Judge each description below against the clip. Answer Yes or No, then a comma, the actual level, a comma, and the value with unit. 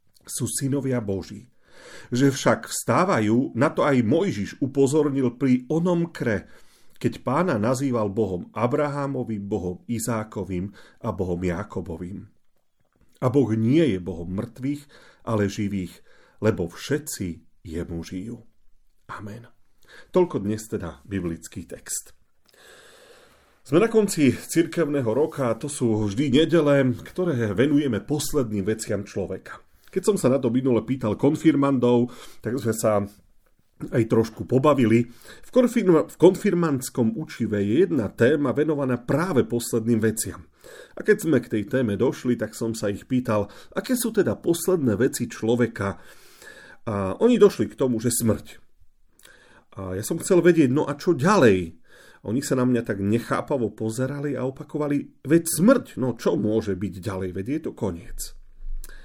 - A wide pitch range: Yes, wide, 5.7 semitones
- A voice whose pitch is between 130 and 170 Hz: No, low, 120 Hz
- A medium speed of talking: Yes, average, 140 wpm